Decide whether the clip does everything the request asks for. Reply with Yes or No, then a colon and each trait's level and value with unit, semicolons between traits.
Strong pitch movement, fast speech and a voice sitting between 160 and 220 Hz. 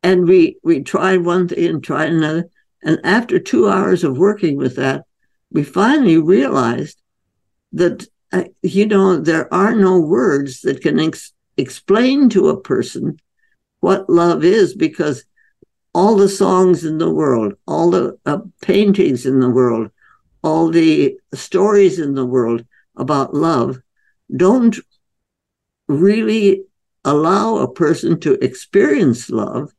No: wide, 6.5 semitones; slow, 135 wpm; medium, 185 Hz